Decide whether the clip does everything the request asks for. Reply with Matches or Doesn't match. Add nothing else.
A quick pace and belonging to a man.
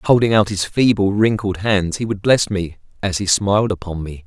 Matches